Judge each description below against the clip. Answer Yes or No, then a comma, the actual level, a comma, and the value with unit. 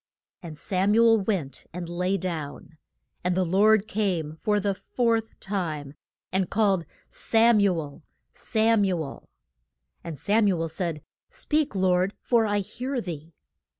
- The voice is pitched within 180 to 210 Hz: Yes, high, 190 Hz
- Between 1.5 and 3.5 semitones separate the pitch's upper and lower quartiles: No, average, 4.4 semitones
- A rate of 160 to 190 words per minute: No, average, 150 wpm